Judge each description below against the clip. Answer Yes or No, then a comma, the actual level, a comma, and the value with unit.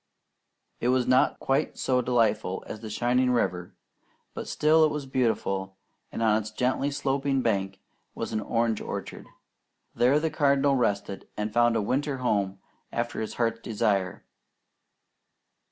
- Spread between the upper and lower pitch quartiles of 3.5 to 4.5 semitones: Yes, average, 4.0 semitones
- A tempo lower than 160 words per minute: Yes, average, 145 wpm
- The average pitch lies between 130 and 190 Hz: No, low, 120 Hz